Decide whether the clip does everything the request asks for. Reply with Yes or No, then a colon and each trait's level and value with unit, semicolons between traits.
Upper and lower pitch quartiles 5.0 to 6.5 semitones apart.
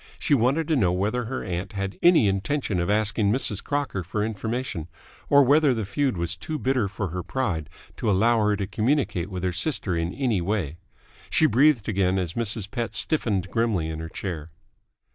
Yes: wide, 5.6 semitones